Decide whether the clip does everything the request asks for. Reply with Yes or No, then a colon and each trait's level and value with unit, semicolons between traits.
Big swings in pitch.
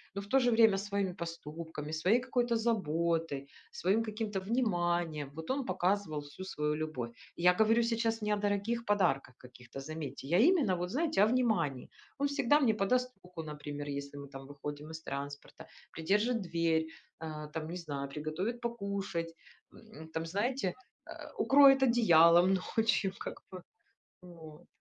Yes: wide, 6.3 semitones